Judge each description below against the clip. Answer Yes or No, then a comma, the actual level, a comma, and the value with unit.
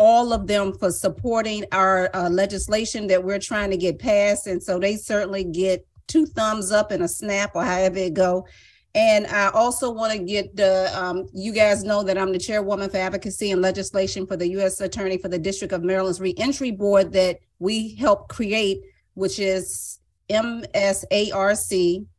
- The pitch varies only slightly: Yes, narrow, 2.2 semitones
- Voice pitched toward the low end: No, high, 195 Hz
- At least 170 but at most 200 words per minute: Yes, average, 180 wpm